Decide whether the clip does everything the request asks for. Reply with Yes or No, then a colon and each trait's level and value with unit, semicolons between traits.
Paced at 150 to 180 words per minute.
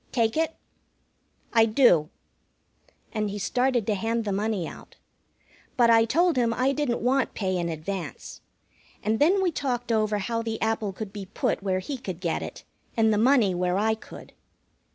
Yes: average, 175 wpm